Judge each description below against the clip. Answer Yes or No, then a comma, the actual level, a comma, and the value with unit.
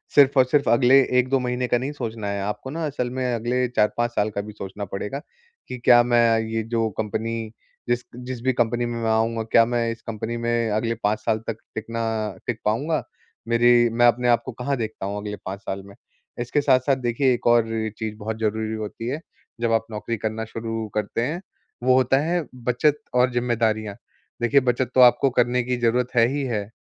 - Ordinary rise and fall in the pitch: No, narrow, 2.2 semitones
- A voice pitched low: Yes, low, 120 Hz